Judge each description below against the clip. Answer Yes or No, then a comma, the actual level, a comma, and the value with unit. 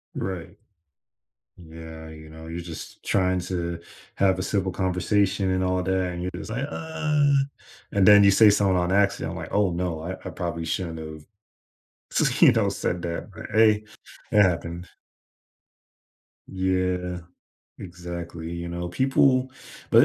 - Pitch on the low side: Yes, very low, 90 Hz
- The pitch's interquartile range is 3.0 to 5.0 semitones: No, narrow, 2.6 semitones